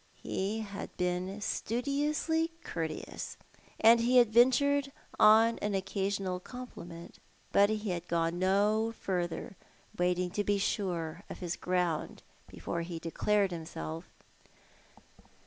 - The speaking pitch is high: Yes, high, 195 Hz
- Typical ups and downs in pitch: Yes, average, 4.3 semitones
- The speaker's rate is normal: No, slow, 115 wpm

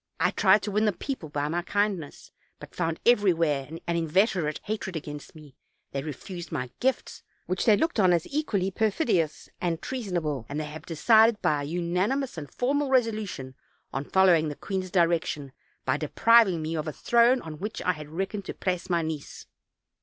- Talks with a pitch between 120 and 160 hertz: No, medium, 175 Hz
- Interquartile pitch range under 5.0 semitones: No, wide, 5.4 semitones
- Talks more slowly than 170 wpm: No, average, 185 wpm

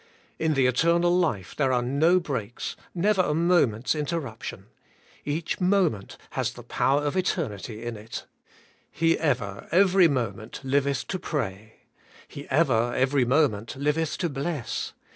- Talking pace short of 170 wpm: Yes, average, 140 wpm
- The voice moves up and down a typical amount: No, wide, 5.8 semitones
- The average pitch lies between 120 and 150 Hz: Yes, medium, 140 Hz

